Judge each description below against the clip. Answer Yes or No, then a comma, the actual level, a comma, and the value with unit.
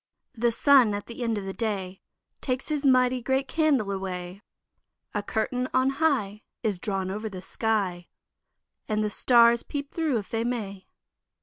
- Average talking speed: Yes, average, 165 wpm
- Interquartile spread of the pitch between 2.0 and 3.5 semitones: No, average, 4.5 semitones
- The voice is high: Yes, high, 225 Hz